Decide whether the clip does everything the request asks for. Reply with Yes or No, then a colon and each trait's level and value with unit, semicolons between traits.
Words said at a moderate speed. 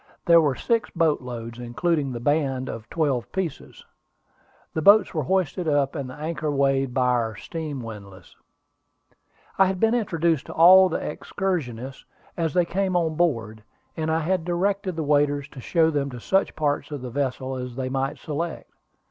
Yes: average, 175 wpm